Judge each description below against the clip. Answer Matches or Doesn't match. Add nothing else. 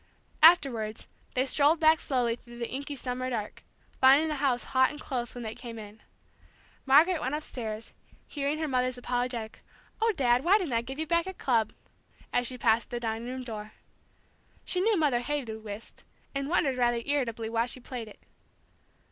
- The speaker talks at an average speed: Matches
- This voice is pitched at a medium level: Doesn't match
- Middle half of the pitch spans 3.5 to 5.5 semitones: Matches